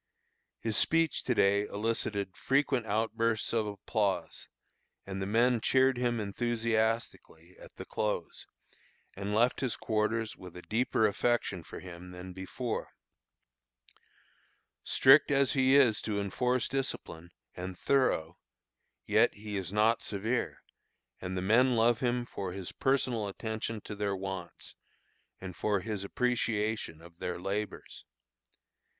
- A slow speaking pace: Yes, slow, 130 wpm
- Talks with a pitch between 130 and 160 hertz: No, low, 110 Hz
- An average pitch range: Yes, average, 3.8 semitones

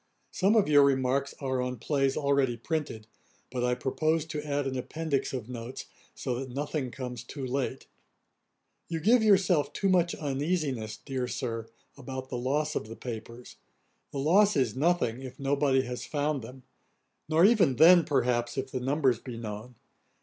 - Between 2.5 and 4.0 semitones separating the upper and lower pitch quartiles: Yes, average, 3.5 semitones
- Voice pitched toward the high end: No, low, 135 Hz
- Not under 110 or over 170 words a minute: Yes, average, 165 wpm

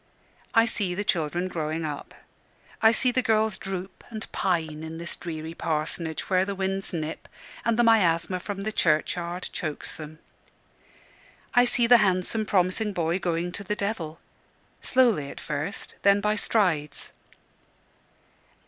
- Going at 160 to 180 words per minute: No, average, 145 wpm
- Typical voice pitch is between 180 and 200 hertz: Yes, medium, 185 Hz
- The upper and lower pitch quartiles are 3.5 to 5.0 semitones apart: Yes, average, 4.4 semitones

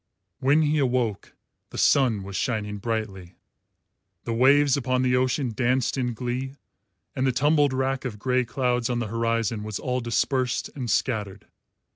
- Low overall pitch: Yes, low, 125 Hz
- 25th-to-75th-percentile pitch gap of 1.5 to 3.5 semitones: Yes, average, 2.8 semitones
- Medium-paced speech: Yes, average, 155 wpm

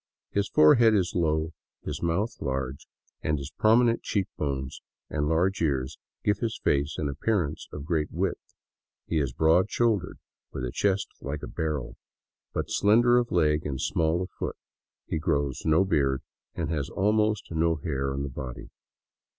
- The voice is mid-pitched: No, very low, 80 Hz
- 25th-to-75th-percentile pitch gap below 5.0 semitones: No, wide, 5.5 semitones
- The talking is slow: No, average, 165 wpm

